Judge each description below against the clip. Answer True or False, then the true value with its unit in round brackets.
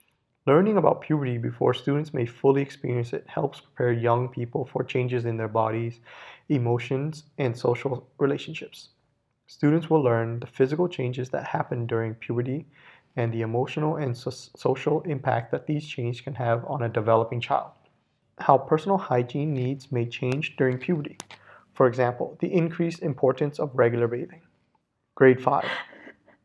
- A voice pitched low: True (130 Hz)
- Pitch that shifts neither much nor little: True (3.4 semitones)